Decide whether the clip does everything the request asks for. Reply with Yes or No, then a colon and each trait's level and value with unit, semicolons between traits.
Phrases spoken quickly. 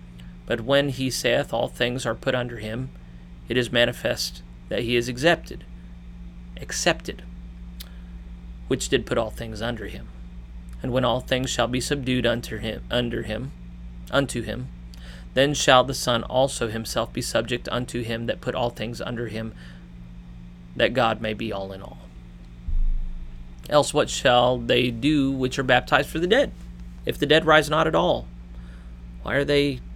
No: average, 165 wpm